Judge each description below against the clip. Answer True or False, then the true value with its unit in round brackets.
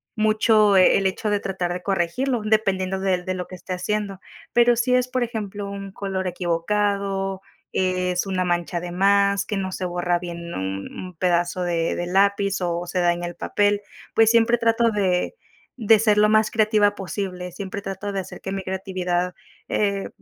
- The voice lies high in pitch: True (195 Hz)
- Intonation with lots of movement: False (2.5 semitones)